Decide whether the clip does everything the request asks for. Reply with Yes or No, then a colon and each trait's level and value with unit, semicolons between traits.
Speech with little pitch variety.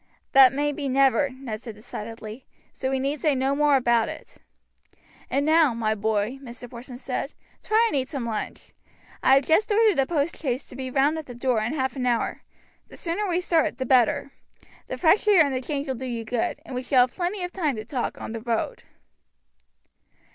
No: average, 3.7 semitones